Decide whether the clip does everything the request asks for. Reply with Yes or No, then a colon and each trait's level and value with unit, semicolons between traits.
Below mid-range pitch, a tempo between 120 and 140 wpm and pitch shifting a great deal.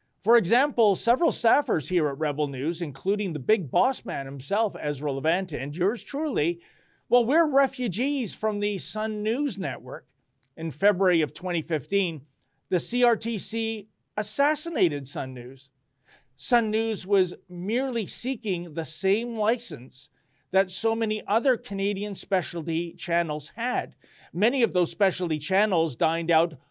No: high, 190 Hz; slow, 135 wpm; wide, 6.1 semitones